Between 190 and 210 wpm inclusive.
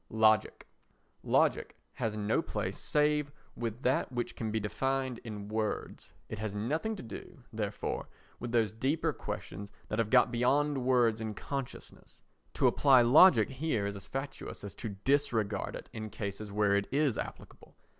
No: average, 160 wpm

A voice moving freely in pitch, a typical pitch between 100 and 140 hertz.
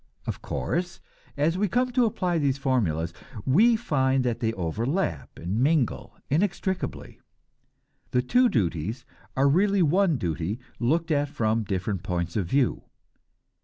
Yes: wide, 9.0 semitones; low, 135 Hz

